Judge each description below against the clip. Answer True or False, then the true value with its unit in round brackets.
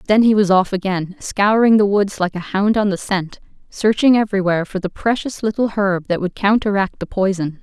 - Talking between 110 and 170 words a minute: False (205 wpm)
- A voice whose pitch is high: True (200 Hz)